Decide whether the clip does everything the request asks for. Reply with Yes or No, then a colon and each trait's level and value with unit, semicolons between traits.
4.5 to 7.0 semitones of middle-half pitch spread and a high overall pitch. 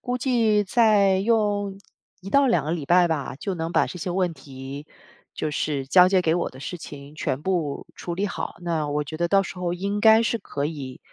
No: average, 5.2 semitones; medium, 175 Hz